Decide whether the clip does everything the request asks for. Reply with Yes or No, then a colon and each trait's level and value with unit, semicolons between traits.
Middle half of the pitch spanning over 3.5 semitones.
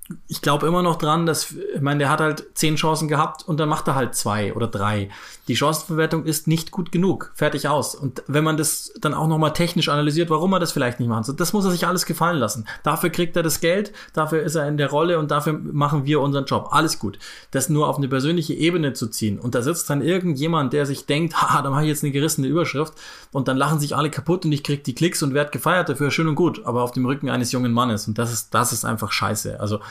No: average, 2.9 semitones